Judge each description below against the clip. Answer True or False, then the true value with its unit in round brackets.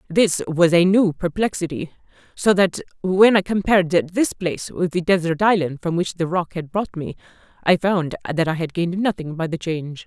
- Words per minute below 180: False (195 wpm)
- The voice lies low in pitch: False (175 Hz)